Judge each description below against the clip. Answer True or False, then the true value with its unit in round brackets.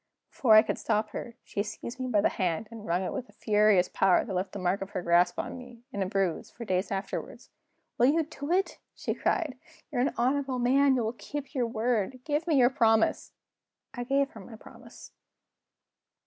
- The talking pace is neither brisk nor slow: False (210 wpm)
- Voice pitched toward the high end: True (230 Hz)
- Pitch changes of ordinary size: True (4.6 semitones)